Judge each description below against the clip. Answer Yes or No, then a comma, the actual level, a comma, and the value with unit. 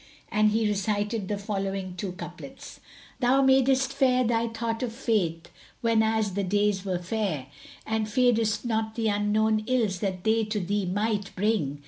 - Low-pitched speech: No, high, 215 Hz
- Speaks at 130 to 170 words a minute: Yes, average, 155 wpm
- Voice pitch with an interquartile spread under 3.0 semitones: Yes, narrow, 2.5 semitones